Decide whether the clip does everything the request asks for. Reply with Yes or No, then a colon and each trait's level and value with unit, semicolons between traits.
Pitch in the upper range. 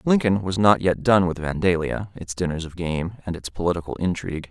No: very low, 90 Hz